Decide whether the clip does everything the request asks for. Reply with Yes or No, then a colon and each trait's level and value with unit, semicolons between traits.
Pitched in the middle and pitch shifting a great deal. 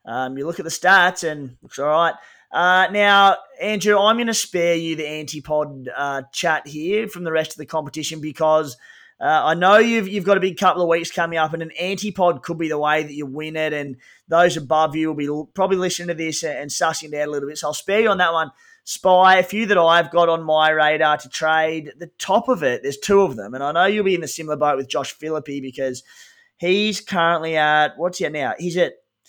No: medium, 165 Hz; average, 3.8 semitones